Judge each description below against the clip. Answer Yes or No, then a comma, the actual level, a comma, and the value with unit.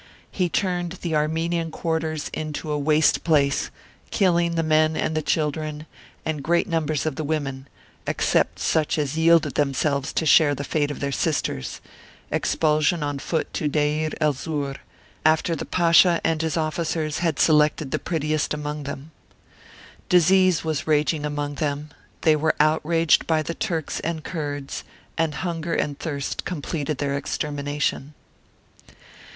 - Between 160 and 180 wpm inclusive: No, average, 145 wpm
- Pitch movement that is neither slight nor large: No, narrow, 1.9 semitones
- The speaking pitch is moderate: Yes, medium, 155 Hz